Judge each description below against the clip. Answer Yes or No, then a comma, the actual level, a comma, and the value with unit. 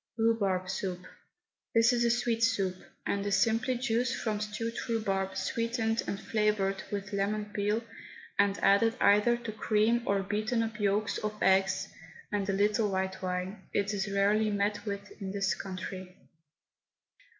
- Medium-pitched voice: No, high, 205 Hz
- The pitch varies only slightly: Yes, narrow, 2.3 semitones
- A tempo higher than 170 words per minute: No, average, 150 wpm